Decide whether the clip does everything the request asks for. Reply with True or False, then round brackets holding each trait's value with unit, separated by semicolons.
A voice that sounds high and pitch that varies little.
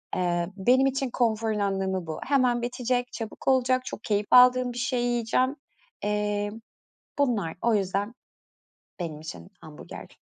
False (225 Hz; 4.2 semitones)